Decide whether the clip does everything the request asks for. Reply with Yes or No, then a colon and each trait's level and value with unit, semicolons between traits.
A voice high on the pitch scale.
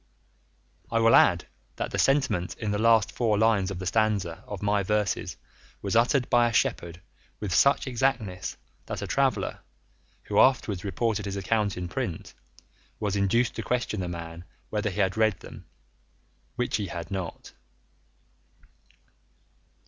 No: low, 105 Hz